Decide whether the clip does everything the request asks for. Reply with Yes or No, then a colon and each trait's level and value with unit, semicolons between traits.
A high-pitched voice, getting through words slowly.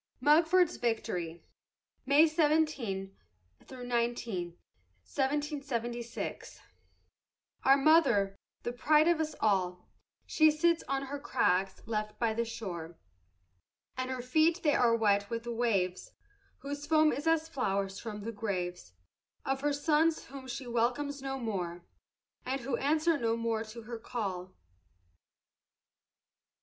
Yes: high, 240 Hz; slow, 120 wpm